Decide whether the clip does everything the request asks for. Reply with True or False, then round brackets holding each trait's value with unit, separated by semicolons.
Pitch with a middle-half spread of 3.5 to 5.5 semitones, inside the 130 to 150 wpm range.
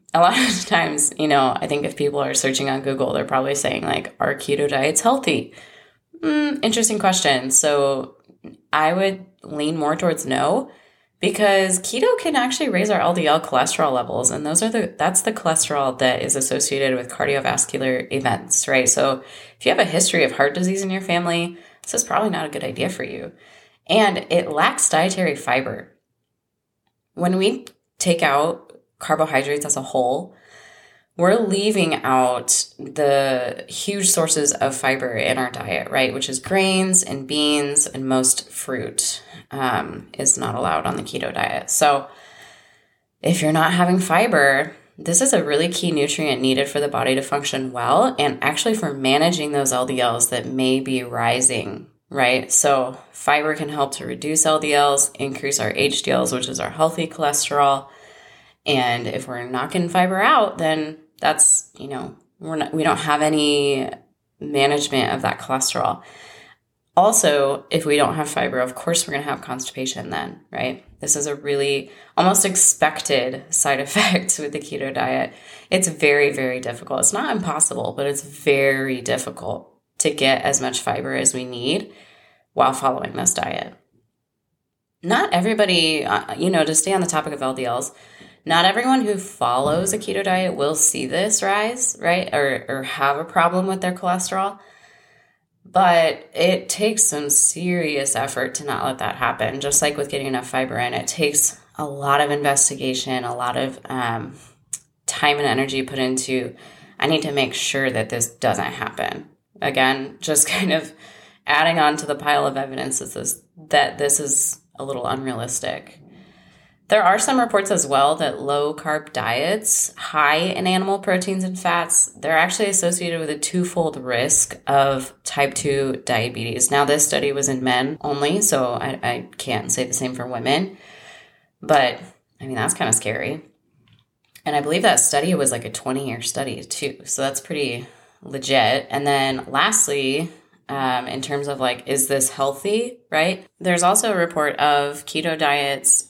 False (4.3 semitones; 170 wpm)